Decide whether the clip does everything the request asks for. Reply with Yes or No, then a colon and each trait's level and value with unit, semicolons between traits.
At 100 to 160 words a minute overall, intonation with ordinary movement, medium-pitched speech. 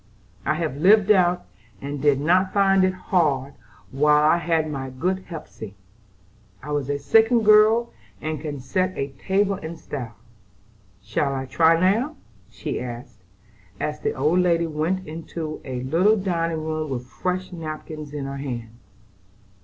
Yes: average, 150 wpm; average, 4.9 semitones; medium, 160 Hz